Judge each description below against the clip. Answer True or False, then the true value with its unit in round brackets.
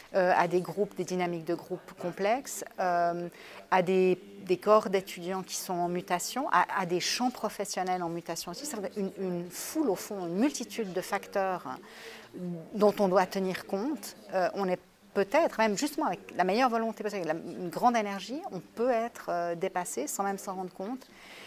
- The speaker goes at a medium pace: True (185 wpm)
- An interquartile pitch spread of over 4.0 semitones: False (3.3 semitones)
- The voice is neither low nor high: False (195 Hz)